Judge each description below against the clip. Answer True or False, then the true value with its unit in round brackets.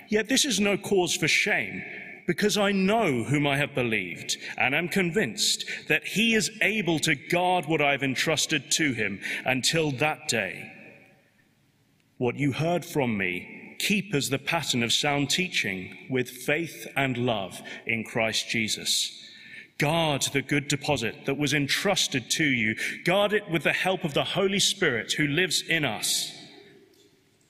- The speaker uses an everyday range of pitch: False (6.1 semitones)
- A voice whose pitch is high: False (150 Hz)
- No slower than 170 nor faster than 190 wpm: False (160 wpm)